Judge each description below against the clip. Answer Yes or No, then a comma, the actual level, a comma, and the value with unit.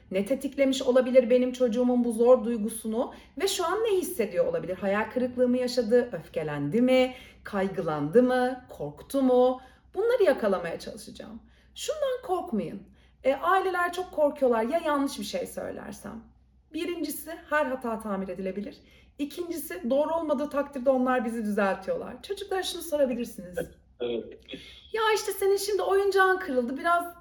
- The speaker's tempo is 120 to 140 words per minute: Yes, average, 130 wpm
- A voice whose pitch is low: No, very high, 265 Hz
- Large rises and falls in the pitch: Yes, wide, 6.4 semitones